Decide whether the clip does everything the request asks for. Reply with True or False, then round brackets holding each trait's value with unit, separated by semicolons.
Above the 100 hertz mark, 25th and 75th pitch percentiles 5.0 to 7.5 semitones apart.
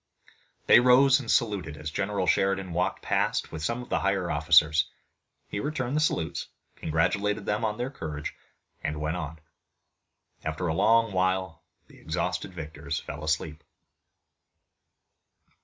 False (90 Hz; 5.4 semitones)